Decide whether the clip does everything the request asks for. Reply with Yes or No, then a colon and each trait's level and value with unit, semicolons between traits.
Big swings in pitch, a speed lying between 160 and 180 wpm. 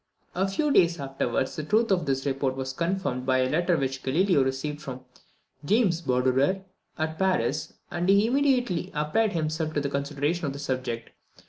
Yes: wide, 5.8 semitones; average, 170 wpm